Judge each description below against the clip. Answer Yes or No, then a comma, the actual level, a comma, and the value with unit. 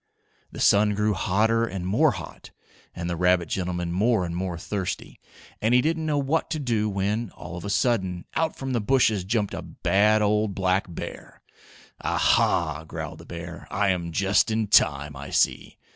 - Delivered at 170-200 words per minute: Yes, average, 185 wpm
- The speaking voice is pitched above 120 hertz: No, low, 100 Hz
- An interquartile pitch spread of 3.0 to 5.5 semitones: Yes, average, 3.9 semitones